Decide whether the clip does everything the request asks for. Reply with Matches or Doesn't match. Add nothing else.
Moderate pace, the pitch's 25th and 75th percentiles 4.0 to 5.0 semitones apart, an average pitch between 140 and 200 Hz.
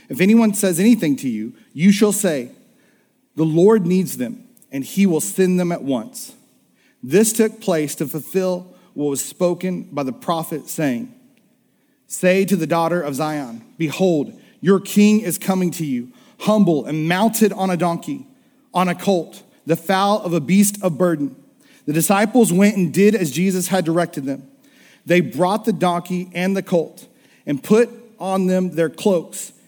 Matches